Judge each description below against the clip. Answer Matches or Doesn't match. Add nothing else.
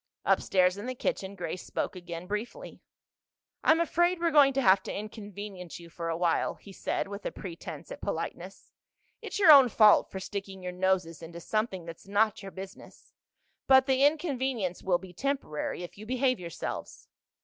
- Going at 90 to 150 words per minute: Doesn't match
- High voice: Matches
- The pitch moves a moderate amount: Doesn't match